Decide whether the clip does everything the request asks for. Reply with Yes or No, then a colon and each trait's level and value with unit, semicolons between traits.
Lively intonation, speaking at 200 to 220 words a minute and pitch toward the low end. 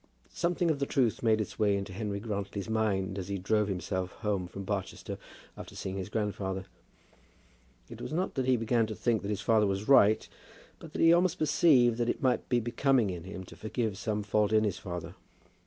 No: average, 3.7 semitones; fast, 205 wpm; low, 105 Hz